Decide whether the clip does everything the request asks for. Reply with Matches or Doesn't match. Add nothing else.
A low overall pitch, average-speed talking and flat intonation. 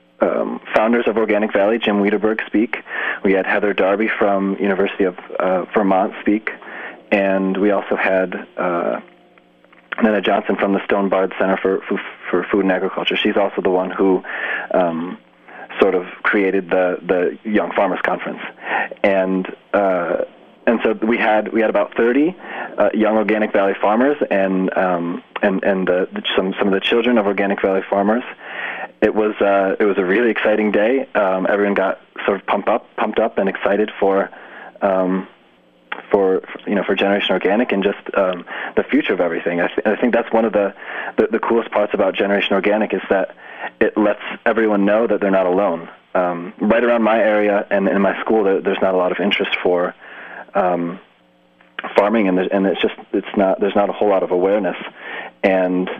Matches